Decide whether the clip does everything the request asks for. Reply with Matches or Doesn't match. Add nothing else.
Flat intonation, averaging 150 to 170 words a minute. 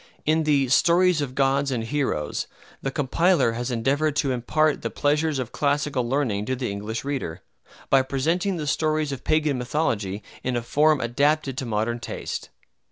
Doesn't match